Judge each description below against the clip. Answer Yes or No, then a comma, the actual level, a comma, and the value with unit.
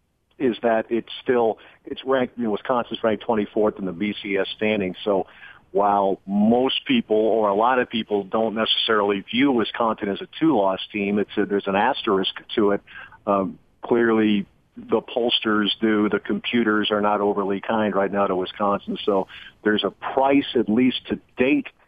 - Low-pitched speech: Yes, low, 105 Hz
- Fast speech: No, average, 175 wpm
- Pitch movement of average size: No, narrow, 2.2 semitones